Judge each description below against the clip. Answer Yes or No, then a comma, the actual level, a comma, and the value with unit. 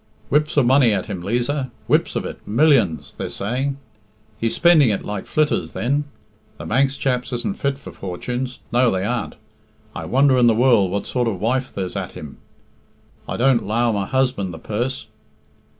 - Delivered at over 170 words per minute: Yes, average, 180 wpm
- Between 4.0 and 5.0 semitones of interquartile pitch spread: Yes, average, 4.6 semitones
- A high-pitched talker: No, low, 120 Hz